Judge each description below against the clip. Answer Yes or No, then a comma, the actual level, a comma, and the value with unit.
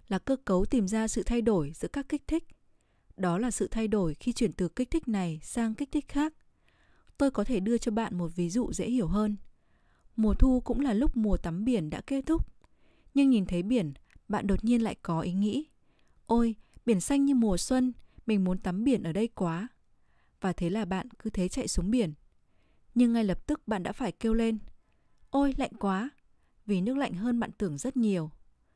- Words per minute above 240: No, average, 215 wpm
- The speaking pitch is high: Yes, high, 225 Hz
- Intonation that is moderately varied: Yes, average, 4.7 semitones